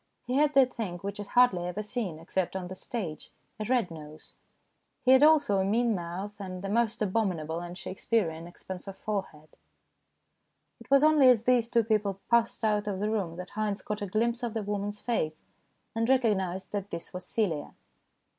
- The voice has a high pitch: Yes, high, 205 Hz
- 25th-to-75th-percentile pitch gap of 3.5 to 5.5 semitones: Yes, average, 4.2 semitones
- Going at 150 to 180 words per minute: No, average, 195 wpm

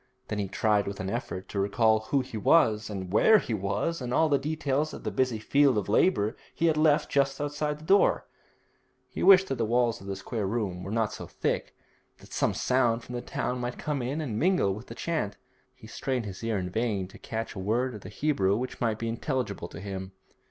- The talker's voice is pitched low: Yes, low, 115 Hz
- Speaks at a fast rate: Yes, fast, 230 wpm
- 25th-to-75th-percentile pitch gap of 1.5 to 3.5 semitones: No, average, 5.2 semitones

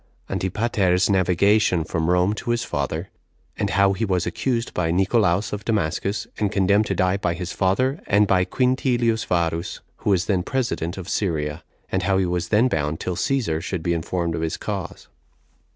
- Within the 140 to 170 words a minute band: No, average, 180 wpm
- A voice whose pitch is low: Yes, very low, 95 Hz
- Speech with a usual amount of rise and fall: Yes, average, 3.5 semitones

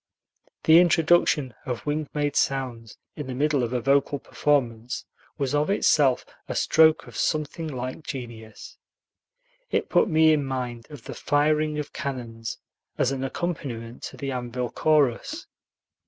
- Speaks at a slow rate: No, average, 145 wpm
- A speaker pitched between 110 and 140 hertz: Yes, low, 135 Hz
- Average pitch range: Yes, average, 3.8 semitones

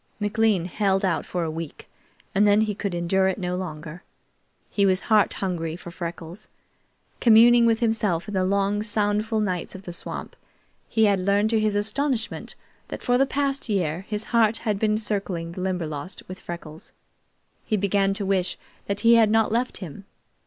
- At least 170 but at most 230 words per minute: Yes, average, 180 wpm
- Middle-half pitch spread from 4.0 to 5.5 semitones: No, average, 3.3 semitones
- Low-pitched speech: No, high, 200 Hz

